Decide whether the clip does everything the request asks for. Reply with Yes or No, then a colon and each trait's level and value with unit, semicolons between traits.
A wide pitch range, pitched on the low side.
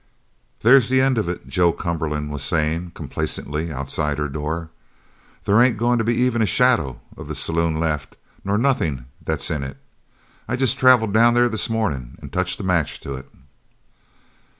Yes: wide, 7.7 semitones; very low, 85 Hz